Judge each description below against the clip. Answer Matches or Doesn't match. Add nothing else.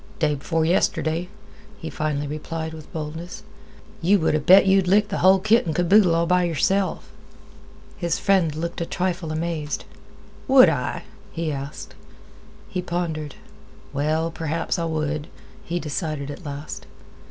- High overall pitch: Doesn't match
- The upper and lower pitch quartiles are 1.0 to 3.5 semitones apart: Matches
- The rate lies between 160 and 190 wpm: Doesn't match